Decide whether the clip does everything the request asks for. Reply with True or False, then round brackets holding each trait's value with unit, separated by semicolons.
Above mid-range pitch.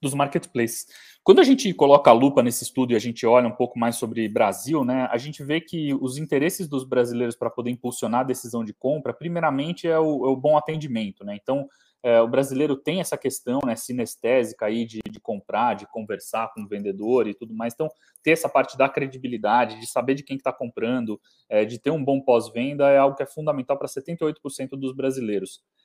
False (130 Hz)